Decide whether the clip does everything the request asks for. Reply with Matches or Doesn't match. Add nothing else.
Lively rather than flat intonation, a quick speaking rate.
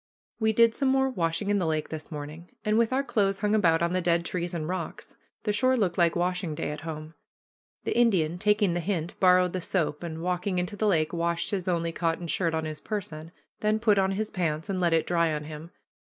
Doesn't match